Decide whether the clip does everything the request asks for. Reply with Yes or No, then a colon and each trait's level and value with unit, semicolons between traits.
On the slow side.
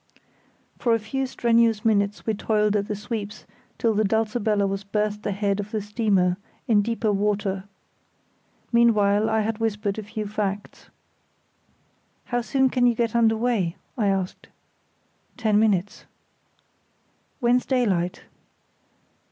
Yes: slow, 130 wpm